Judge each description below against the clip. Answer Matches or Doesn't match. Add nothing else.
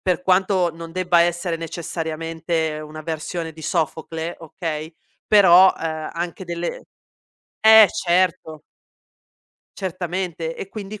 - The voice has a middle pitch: Matches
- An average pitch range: Doesn't match